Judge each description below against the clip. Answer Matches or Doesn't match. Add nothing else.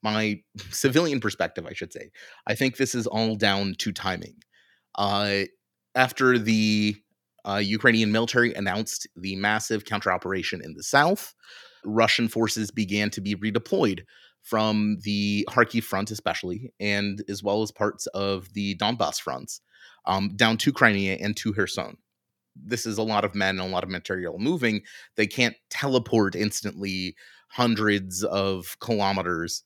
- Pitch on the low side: Matches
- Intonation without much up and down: Matches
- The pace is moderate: Matches